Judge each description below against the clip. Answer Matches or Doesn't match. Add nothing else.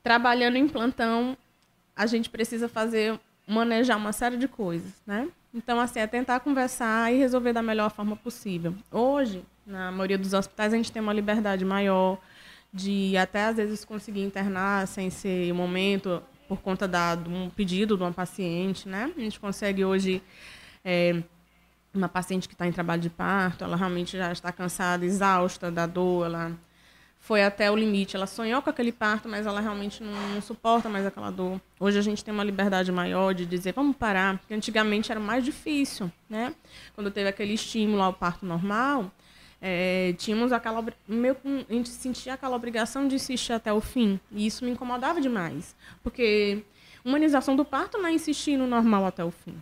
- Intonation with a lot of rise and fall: Doesn't match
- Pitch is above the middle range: Matches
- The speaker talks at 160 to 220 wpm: Matches